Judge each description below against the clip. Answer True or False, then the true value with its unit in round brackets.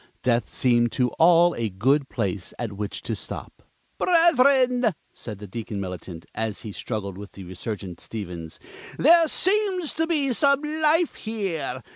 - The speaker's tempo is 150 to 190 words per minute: False (140 wpm)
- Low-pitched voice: True (125 Hz)